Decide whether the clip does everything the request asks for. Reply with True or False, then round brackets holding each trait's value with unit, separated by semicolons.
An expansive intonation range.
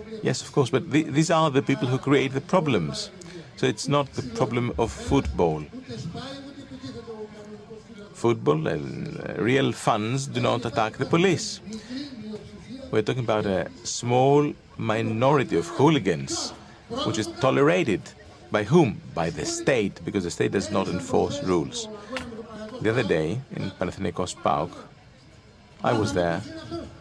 True (8.9 semitones)